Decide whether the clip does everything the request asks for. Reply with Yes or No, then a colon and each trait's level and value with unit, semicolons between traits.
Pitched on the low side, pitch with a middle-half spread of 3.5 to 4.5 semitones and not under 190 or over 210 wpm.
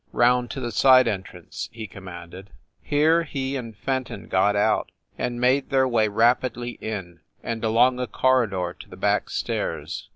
No: low, 120 Hz; average, 4.0 semitones; average, 160 wpm